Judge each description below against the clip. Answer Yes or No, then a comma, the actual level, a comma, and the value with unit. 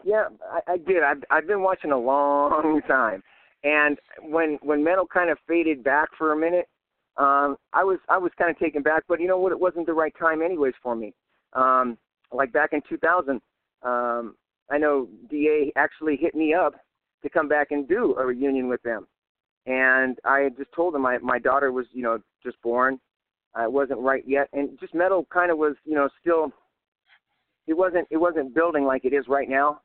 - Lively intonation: No, average, 3.6 semitones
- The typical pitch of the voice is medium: Yes, medium, 145 Hz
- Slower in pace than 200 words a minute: No, fast, 205 wpm